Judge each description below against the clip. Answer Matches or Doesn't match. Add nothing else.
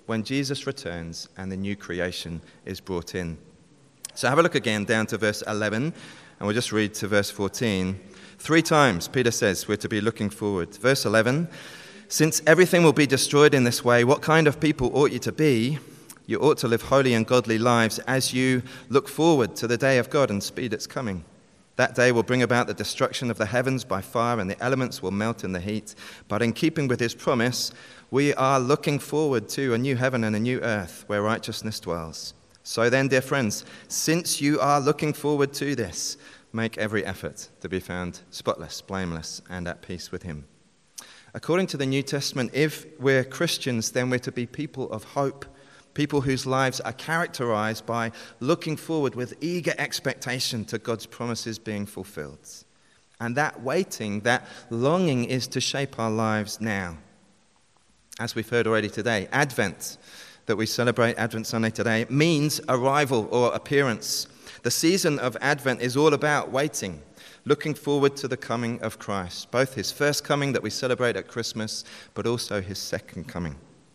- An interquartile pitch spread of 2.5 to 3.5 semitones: Doesn't match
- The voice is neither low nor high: Doesn't match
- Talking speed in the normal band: Matches